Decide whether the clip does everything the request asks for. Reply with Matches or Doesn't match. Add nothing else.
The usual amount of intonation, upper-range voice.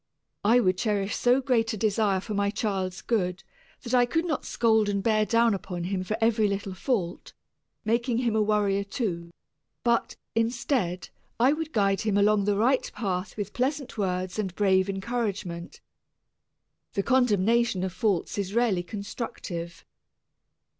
Matches